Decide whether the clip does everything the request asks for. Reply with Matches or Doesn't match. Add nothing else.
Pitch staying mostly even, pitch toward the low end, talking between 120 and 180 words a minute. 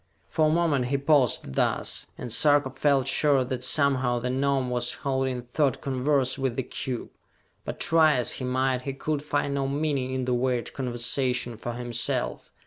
Matches